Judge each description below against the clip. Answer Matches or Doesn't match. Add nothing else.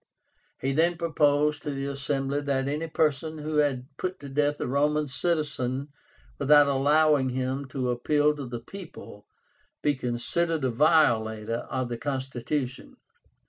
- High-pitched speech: Doesn't match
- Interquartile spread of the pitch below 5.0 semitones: Matches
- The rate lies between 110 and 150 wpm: Matches